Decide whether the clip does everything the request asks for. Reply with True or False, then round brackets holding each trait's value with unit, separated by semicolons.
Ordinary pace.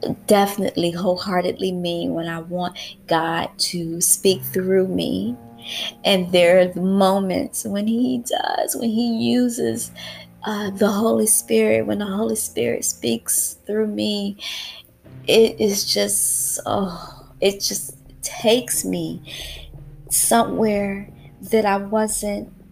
False (120 wpm)